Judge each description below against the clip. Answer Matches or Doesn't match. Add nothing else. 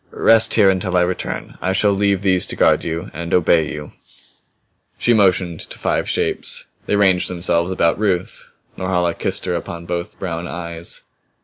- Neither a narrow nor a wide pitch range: Doesn't match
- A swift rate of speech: Doesn't match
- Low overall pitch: Matches